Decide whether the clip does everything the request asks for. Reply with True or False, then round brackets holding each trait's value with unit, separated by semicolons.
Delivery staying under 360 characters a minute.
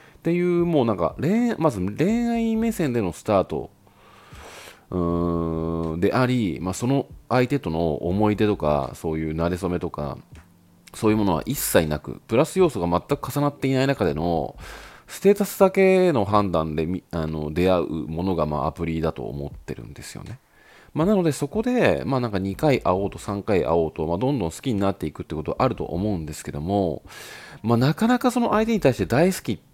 False (365 characters per minute)